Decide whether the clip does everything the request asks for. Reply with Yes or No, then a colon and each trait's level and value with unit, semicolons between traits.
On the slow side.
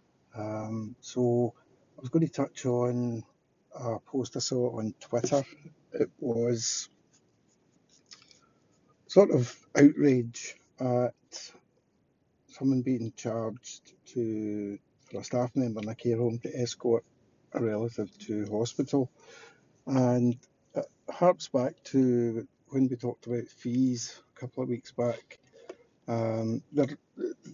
Yes: slow, 120 wpm